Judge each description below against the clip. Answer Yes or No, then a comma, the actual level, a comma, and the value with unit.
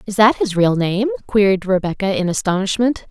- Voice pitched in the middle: No, high, 205 Hz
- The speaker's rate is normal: Yes, average, 175 wpm